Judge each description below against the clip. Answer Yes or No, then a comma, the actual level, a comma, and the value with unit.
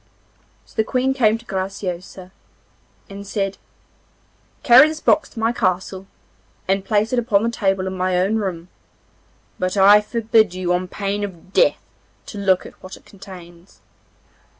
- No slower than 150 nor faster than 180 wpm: Yes, average, 155 wpm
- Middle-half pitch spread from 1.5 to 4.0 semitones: Yes, average, 2.9 semitones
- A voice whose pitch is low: No, high, 195 Hz